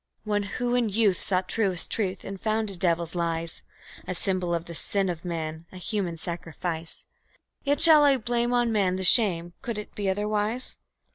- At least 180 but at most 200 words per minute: Yes, average, 185 wpm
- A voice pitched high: Yes, high, 195 Hz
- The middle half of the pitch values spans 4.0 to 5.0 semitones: Yes, average, 4.3 semitones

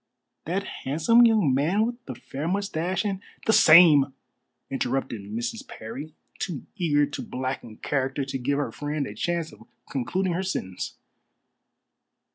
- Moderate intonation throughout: No, wide, 5.9 semitones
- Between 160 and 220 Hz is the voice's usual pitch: No, medium, 150 Hz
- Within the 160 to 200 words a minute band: No, average, 145 wpm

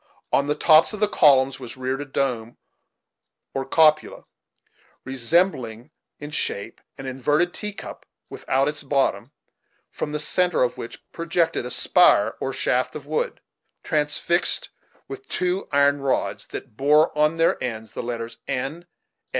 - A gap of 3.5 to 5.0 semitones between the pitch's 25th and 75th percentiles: Yes, average, 4.1 semitones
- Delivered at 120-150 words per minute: Yes, average, 145 wpm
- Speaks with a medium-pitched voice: Yes, medium, 145 Hz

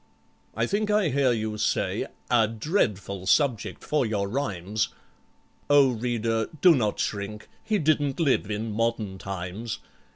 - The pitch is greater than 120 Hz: No, low, 115 Hz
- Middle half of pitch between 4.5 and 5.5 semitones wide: Yes, average, 5.2 semitones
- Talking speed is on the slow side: Yes, slow, 130 wpm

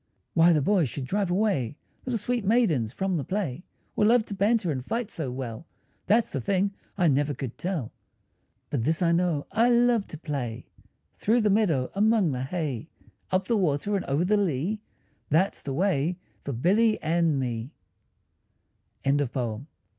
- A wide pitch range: Yes, wide, 6.9 semitones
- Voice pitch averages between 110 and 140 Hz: No, medium, 170 Hz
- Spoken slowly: No, average, 170 wpm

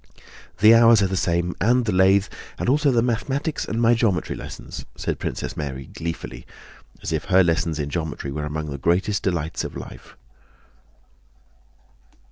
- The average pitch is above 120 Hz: No, very low, 95 Hz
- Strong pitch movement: Yes, wide, 6.2 semitones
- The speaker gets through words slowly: No, average, 165 wpm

